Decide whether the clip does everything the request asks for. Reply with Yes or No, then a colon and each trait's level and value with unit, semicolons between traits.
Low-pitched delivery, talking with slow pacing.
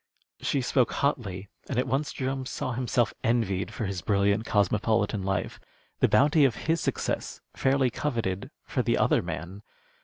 No: low, 115 Hz; average, 155 wpm